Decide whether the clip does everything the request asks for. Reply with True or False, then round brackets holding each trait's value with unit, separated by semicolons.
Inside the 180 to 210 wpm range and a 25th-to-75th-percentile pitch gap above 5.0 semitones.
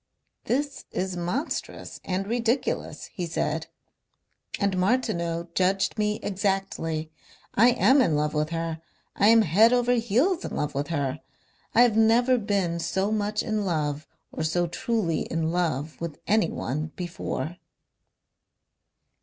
False (135 wpm; 5.4 semitones)